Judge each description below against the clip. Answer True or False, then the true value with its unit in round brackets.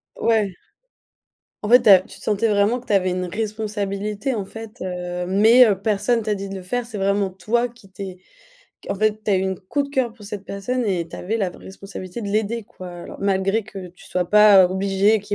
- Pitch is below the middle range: False (200 Hz)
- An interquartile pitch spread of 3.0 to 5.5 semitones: False (2.5 semitones)